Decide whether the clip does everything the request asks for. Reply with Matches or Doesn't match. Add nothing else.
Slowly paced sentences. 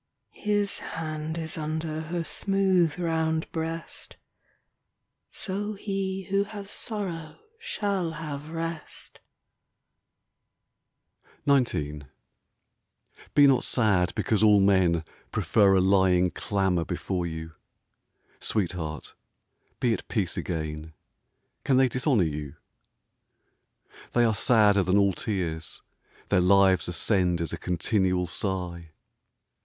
Matches